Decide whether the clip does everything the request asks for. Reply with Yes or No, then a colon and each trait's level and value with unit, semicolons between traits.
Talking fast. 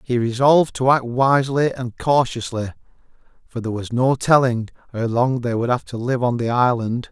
No: average, 185 wpm